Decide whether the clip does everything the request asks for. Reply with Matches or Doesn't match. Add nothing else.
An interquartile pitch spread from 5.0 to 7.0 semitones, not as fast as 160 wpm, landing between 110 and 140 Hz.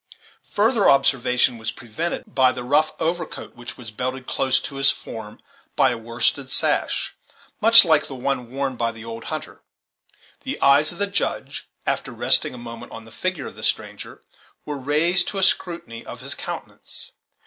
Doesn't match